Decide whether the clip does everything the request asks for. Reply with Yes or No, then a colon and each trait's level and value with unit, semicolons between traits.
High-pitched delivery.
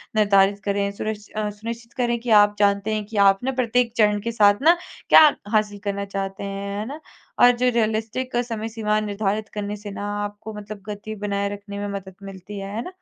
Yes: high, 210 Hz